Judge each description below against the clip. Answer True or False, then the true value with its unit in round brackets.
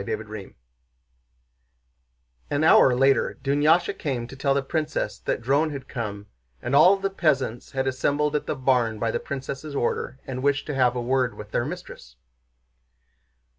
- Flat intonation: False (3.2 semitones)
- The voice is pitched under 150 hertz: True (135 Hz)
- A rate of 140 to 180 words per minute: True (160 wpm)